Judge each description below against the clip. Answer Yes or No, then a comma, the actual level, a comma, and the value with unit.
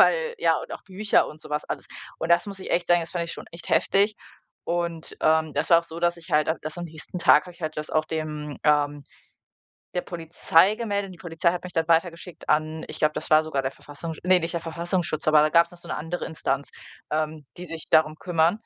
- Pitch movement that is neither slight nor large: No, narrow, 2.2 semitones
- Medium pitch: Yes, medium, 165 Hz